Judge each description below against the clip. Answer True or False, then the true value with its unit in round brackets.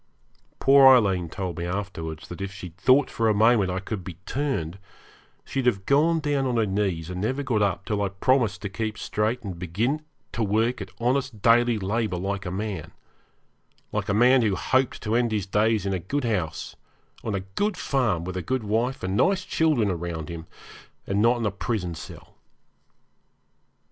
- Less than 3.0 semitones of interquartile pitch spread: False (4.6 semitones)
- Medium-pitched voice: False (105 Hz)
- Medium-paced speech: True (190 wpm)